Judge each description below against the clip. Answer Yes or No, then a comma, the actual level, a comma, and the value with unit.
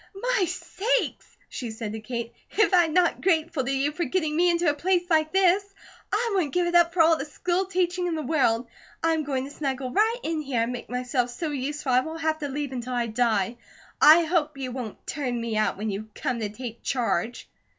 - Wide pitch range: Yes, wide, 5.8 semitones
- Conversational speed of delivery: No, fast, 225 wpm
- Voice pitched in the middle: No, very high, 295 Hz